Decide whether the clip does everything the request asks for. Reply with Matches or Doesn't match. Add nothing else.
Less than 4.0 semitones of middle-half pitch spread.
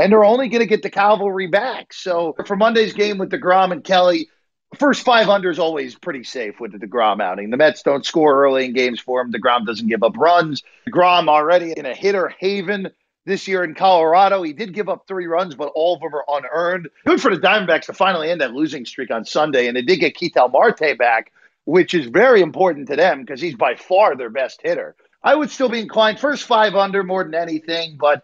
Doesn't match